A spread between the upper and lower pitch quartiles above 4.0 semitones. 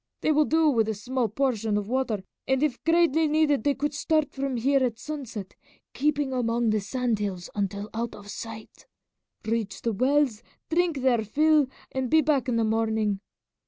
Yes: average, 4.9 semitones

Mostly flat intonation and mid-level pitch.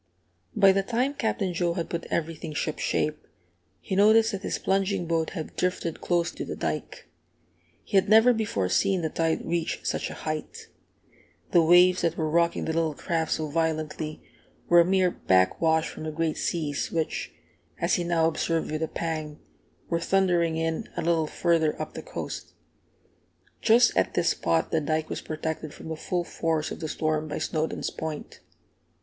Yes: narrow, 2.3 semitones; medium, 165 Hz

